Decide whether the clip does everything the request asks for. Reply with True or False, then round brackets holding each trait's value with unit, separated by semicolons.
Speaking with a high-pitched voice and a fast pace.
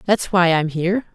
False (180 Hz; 210 wpm)